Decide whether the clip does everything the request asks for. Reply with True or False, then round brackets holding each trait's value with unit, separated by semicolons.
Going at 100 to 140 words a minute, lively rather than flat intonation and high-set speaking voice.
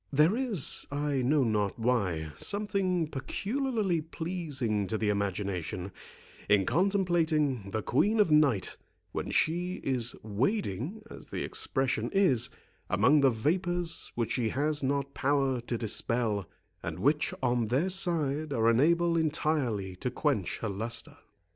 False (135 wpm; 7.0 semitones; 135 Hz)